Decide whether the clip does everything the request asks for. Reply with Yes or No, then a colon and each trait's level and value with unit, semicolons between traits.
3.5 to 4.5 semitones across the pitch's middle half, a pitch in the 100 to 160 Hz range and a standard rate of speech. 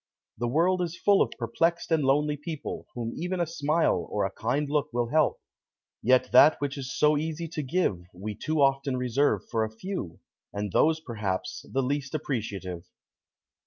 No: average, 5.3 semitones; medium, 140 Hz; average, 175 wpm